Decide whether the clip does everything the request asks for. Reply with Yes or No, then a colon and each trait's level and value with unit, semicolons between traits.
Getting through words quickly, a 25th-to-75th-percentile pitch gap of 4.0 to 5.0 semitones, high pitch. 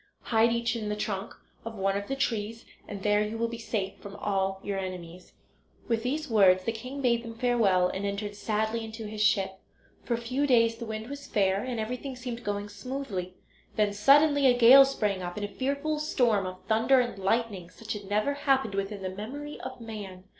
No: fast, 210 wpm; average, 3.6 semitones; high, 220 Hz